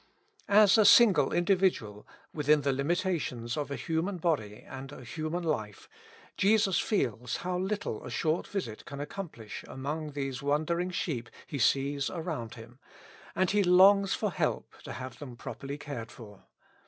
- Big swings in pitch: Yes, wide, 5.9 semitones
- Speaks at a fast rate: No, average, 155 wpm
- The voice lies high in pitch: No, medium, 150 Hz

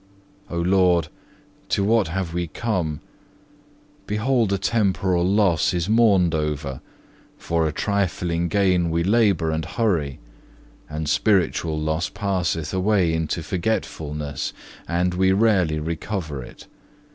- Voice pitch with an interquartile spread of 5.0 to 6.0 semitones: No, average, 3.8 semitones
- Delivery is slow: Yes, slow, 120 wpm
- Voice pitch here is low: Yes, very low, 90 Hz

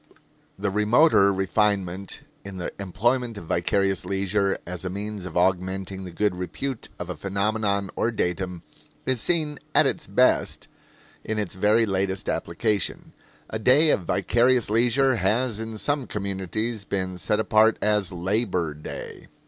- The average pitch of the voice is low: Yes, low, 100 Hz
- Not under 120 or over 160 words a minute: Yes, average, 145 wpm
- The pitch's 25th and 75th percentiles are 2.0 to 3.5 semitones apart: Yes, average, 3.0 semitones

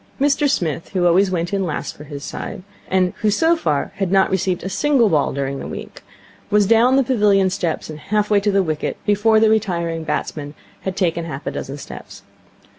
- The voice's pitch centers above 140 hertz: Yes, high, 190 Hz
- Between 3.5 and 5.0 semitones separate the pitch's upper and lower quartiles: Yes, average, 4.3 semitones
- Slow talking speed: No, fast, 205 wpm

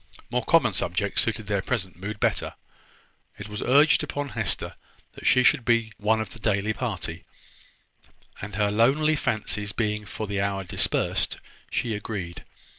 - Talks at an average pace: Yes, average, 155 wpm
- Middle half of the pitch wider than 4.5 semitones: No, average, 2.9 semitones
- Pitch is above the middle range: No, low, 105 Hz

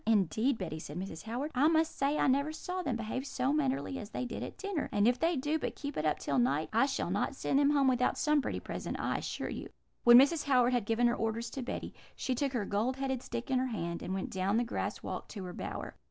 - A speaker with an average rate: No, fast, 260 wpm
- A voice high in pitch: Yes, very high, 250 Hz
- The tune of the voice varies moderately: Yes, average, 4.9 semitones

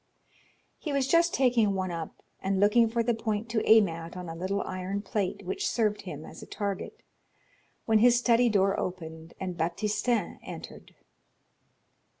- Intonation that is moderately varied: Yes, average, 4.0 semitones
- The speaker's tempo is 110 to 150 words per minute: No, average, 160 wpm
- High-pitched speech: Yes, high, 205 Hz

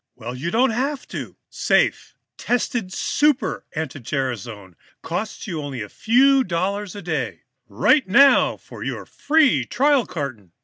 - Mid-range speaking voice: Yes, medium, 180 Hz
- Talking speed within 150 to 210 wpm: No, average, 140 wpm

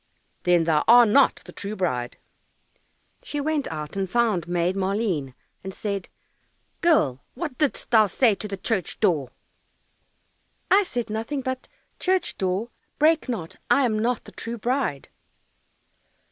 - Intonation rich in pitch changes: Yes, wide, 6.0 semitones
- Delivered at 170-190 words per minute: No, average, 145 wpm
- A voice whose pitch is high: Yes, high, 215 Hz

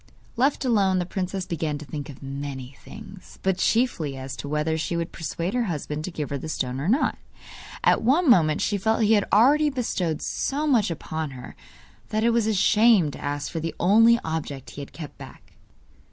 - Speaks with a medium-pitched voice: Yes, medium, 175 Hz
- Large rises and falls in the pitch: Yes, wide, 6.9 semitones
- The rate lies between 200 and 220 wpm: Yes, fast, 205 wpm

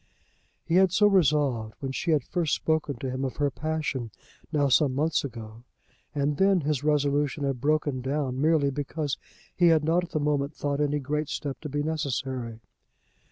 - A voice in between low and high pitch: Yes, medium, 145 Hz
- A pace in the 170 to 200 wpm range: Yes, average, 180 wpm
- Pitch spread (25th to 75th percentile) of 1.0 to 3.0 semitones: Yes, narrow, 2.5 semitones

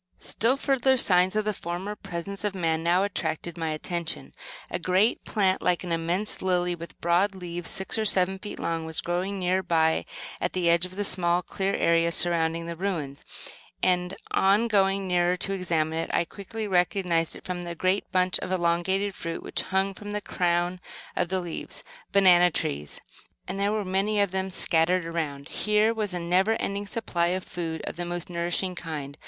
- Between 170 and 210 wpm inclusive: Yes, average, 185 wpm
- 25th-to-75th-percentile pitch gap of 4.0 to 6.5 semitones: No, narrow, 2.4 semitones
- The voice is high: No, medium, 180 Hz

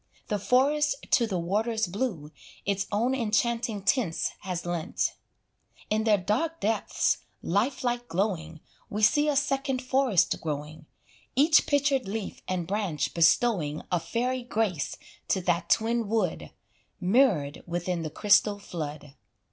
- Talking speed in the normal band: No, slow, 130 wpm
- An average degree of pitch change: No, wide, 6.0 semitones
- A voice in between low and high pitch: No, high, 210 Hz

